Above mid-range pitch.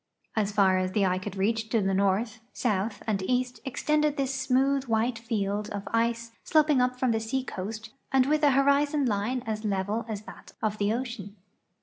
Yes: high, 225 Hz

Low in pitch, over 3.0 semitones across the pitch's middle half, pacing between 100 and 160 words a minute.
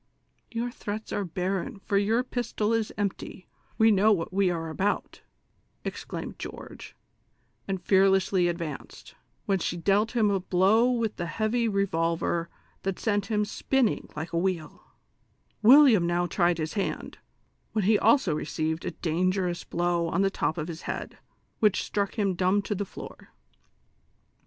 No: high, 195 Hz; average, 3.7 semitones; average, 155 wpm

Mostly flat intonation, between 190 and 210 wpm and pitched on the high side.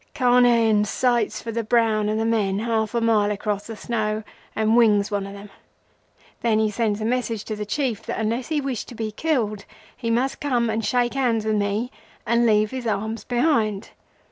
Yes: narrow, 2.2 semitones; average, 195 wpm; high, 225 Hz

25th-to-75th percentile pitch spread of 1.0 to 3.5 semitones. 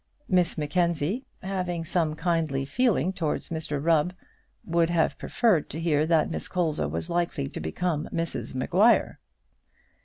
Yes: average, 2.8 semitones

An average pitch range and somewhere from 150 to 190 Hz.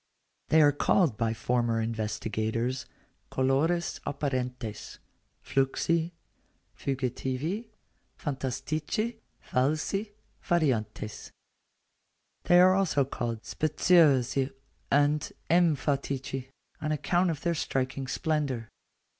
No: average, 4.2 semitones; medium, 140 Hz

